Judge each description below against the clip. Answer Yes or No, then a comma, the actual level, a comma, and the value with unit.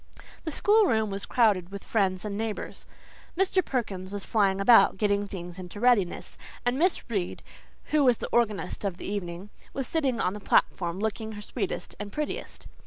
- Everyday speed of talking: Yes, average, 175 wpm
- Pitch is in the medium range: No, high, 210 Hz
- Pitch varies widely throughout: No, average, 4.0 semitones